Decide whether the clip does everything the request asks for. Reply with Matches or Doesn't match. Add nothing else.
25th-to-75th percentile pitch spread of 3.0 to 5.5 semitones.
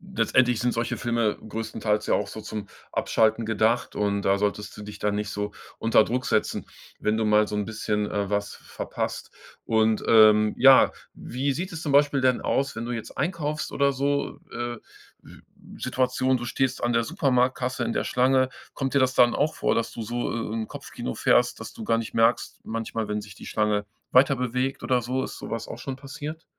Matches